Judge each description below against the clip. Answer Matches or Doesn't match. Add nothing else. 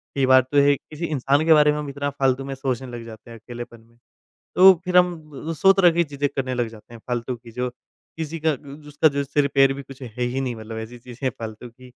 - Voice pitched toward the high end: Doesn't match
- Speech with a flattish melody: Doesn't match